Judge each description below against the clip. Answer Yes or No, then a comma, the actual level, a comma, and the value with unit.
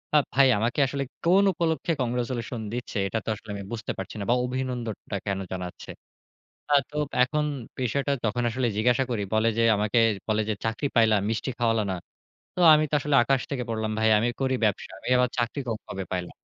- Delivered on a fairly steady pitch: No, average, 3.3 semitones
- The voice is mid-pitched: No, low, 120 Hz